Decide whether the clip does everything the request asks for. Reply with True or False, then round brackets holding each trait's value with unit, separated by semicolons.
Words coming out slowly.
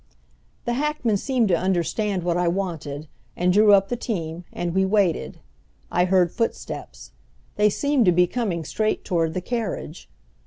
False (160 wpm)